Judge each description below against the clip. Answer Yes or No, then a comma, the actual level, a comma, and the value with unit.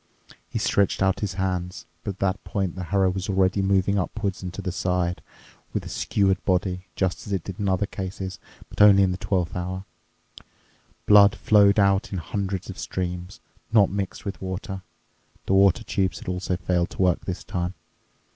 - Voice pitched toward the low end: Yes, very low, 95 Hz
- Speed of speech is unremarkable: Yes, average, 180 wpm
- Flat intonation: Yes, narrow, 1.4 semitones